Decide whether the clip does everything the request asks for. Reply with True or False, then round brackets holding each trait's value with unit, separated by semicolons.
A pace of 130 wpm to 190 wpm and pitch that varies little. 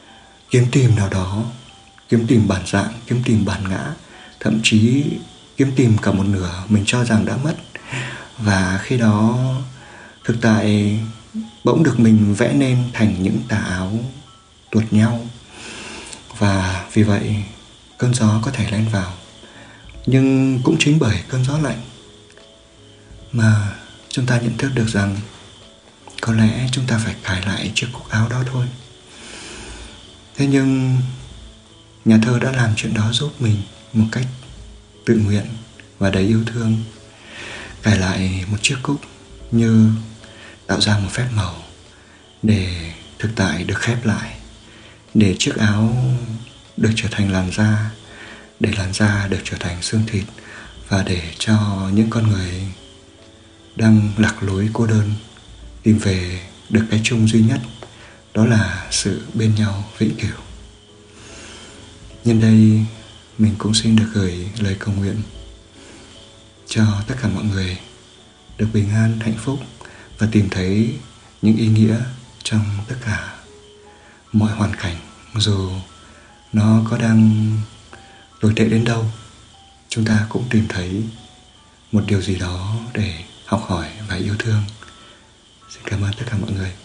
True (145 wpm; 2.0 semitones)